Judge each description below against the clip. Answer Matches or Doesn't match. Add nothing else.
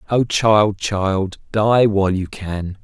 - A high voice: Doesn't match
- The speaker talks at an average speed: Matches